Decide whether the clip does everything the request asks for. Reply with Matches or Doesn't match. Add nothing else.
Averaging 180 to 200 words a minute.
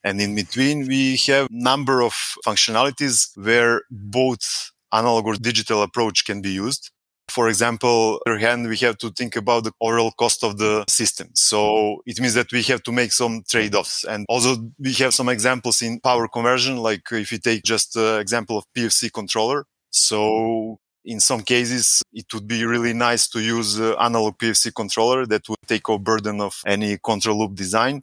Matches